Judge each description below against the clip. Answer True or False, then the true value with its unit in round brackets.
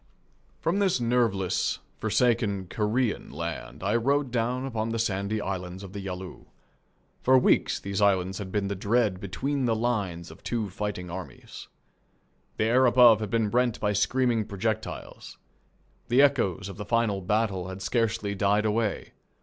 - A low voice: True (105 Hz)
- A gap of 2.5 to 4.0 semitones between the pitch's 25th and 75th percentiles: True (3.4 semitones)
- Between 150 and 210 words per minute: True (155 wpm)